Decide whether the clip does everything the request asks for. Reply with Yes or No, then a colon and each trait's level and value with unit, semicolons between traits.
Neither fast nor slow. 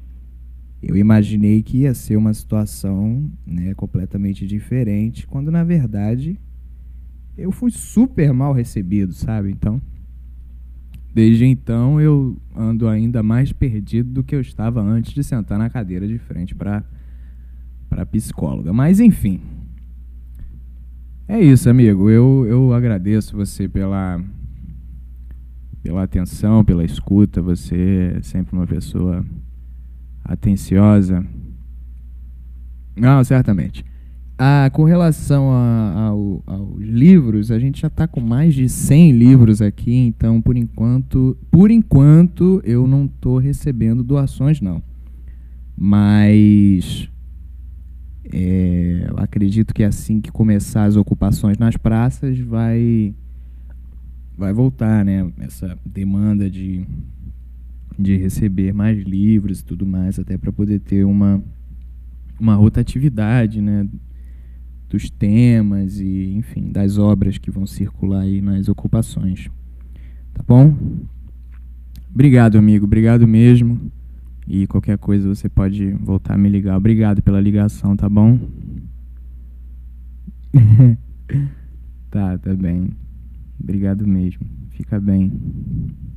No: slow, 115 wpm